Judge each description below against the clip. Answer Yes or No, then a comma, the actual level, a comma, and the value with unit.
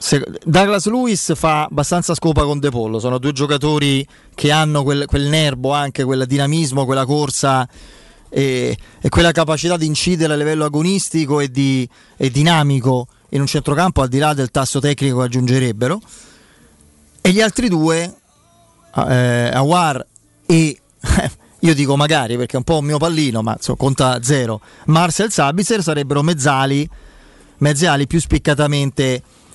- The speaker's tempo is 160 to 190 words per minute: No, average, 145 wpm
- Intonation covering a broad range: No, average, 3.2 semitones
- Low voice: No, medium, 145 Hz